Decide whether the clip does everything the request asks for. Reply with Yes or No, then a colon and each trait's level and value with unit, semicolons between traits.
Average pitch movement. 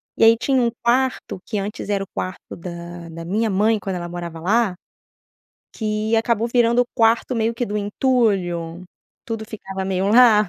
Yes: average, 3.9 semitones